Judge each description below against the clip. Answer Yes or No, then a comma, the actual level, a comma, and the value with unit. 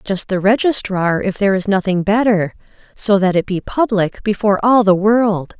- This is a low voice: No, high, 200 Hz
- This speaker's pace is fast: No, average, 170 wpm